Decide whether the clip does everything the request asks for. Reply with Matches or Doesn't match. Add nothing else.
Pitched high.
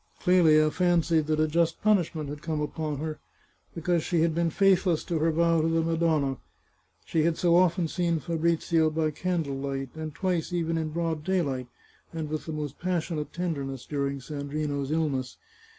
Doesn't match